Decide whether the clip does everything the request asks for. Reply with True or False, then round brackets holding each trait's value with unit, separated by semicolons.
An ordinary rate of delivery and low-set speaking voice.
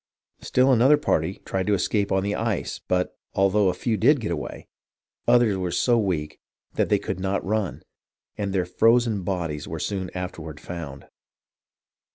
True (160 wpm; 95 Hz)